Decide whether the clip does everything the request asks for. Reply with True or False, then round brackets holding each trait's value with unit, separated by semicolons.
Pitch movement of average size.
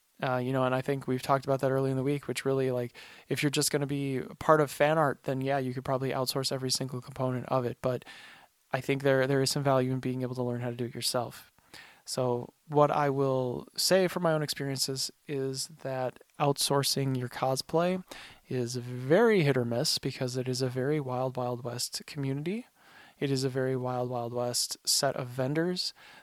False (2.0 semitones)